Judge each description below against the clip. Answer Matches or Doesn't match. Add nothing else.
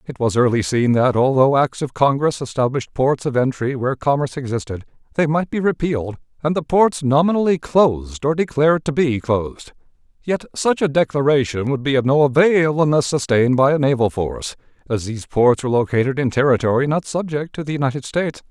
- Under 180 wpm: Doesn't match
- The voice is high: Doesn't match